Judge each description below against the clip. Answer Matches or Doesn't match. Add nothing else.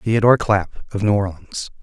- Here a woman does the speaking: Doesn't match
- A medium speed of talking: Matches